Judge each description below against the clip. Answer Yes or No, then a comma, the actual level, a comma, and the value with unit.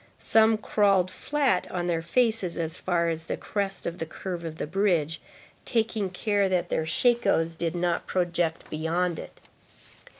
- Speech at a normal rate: Yes, average, 160 wpm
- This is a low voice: No, medium, 180 Hz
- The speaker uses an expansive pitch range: No, average, 3.6 semitones